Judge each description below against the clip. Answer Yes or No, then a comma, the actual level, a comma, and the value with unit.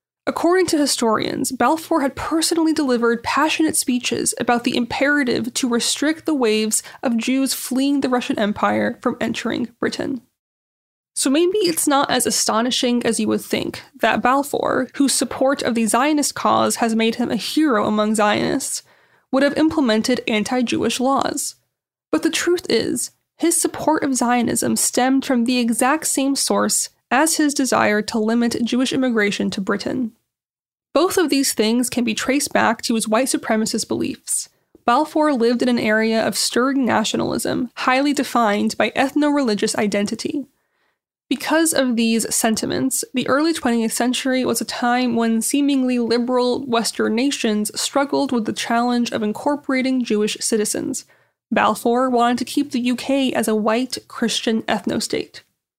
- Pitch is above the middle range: Yes, very high, 250 Hz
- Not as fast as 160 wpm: Yes, average, 150 wpm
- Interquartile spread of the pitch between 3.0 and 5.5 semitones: Yes, average, 3.5 semitones